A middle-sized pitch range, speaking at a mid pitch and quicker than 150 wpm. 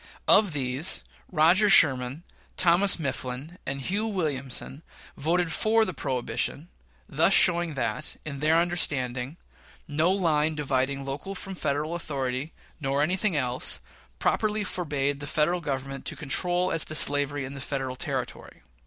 No: average, 4.3 semitones; medium, 150 Hz; slow, 135 wpm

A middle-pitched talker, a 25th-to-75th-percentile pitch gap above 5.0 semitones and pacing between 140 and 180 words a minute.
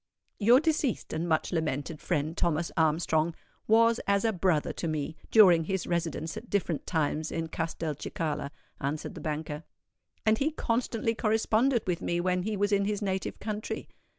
Yes: medium, 175 Hz; wide, 5.4 semitones; average, 160 wpm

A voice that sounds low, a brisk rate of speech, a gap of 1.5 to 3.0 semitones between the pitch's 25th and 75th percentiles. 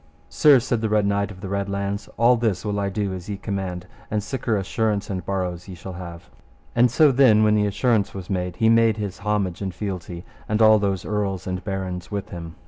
Yes: low, 100 Hz; fast, 225 wpm; narrow, 2.5 semitones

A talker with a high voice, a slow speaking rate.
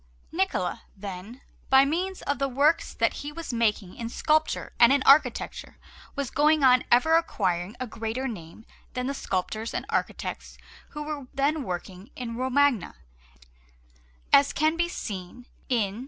No: very high, 255 Hz; average, 155 wpm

